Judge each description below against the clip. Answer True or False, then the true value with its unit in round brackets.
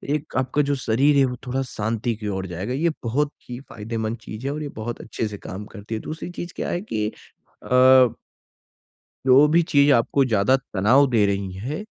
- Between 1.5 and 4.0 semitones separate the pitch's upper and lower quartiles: False (4.7 semitones)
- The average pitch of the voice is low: True (125 Hz)